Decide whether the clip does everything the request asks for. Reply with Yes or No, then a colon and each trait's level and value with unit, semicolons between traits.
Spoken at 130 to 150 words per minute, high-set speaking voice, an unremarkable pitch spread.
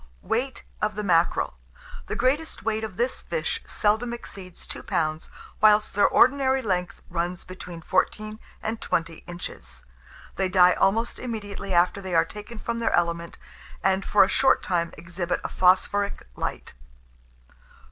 Yes: average, 145 wpm; high, 195 Hz; average, 4.2 semitones